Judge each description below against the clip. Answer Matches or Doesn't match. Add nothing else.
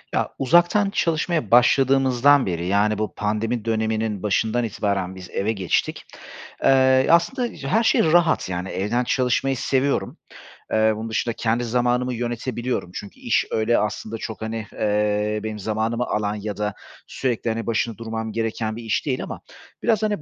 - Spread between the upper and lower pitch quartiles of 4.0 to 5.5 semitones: Doesn't match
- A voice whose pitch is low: Matches